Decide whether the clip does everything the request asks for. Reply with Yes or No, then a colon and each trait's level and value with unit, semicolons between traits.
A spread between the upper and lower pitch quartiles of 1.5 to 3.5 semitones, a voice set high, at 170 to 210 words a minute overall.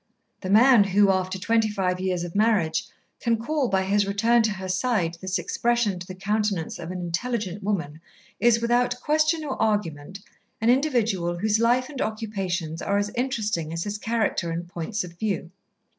No: average, 4.2 semitones; high, 205 Hz; average, 175 wpm